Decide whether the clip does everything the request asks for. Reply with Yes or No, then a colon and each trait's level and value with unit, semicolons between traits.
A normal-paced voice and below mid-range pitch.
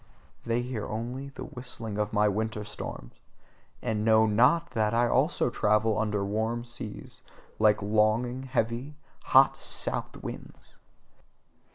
No: slow, 130 wpm; low, 110 Hz